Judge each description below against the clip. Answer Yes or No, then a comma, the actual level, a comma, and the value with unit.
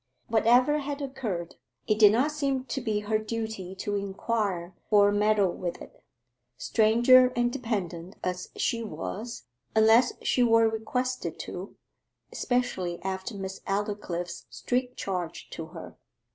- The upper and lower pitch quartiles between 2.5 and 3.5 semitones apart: No, average, 4.2 semitones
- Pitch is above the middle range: Yes, high, 215 Hz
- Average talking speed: No, slow, 130 wpm